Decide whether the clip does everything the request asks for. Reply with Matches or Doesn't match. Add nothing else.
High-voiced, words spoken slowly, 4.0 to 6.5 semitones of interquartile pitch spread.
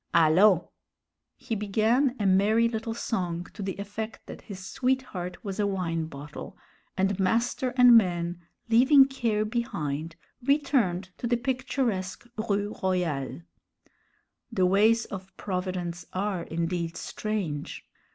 Matches